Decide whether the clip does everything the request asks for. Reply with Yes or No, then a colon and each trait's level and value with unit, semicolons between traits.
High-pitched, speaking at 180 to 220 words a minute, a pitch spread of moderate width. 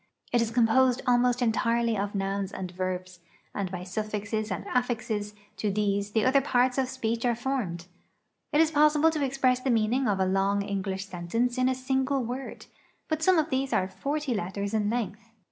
Yes: high, 230 Hz; average, 185 wpm; average, 4.5 semitones